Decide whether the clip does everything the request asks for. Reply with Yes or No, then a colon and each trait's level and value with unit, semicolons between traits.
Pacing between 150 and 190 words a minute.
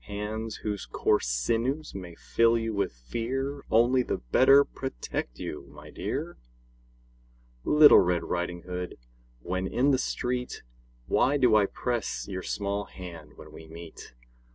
No: average, 140 wpm